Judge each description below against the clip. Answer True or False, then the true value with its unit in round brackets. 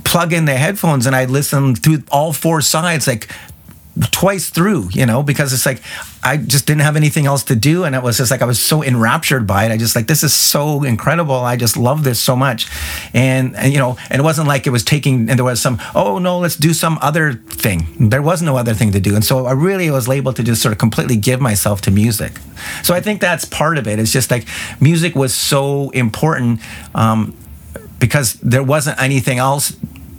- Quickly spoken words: True (230 wpm)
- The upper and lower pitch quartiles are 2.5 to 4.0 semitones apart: False (4.5 semitones)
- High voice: False (135 Hz)